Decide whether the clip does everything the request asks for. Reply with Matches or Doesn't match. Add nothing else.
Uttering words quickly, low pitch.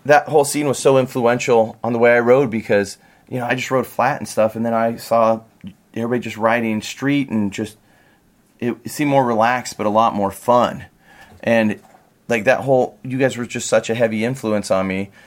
Matches